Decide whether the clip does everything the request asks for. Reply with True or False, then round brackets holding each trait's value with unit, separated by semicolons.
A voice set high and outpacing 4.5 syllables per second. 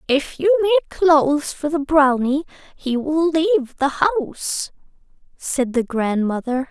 False (295 Hz; 4.1 syllables/s)